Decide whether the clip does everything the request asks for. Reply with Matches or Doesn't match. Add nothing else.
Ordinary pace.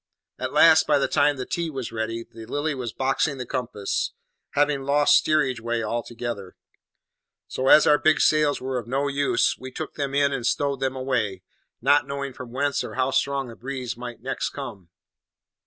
Matches